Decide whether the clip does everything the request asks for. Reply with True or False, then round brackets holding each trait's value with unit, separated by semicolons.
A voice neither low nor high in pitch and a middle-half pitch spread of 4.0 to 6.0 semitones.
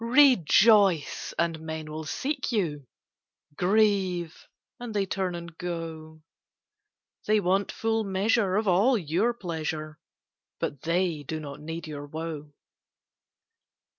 True (175 Hz; 4.7 semitones)